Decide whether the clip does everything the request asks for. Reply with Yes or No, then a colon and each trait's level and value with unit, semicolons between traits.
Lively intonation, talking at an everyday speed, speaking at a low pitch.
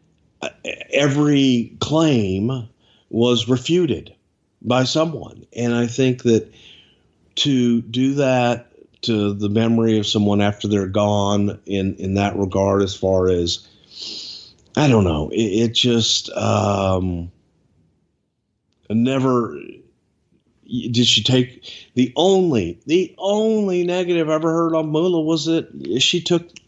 No: wide, 6.2 semitones; slow, 120 wpm; low, 120 Hz